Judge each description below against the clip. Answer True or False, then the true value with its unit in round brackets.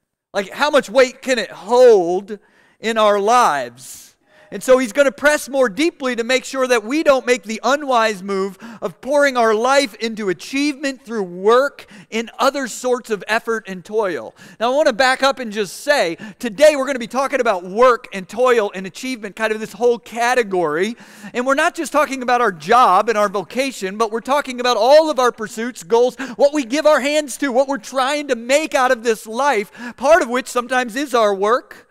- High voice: True (245 Hz)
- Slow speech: False (210 wpm)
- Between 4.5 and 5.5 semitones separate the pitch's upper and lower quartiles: False (4.0 semitones)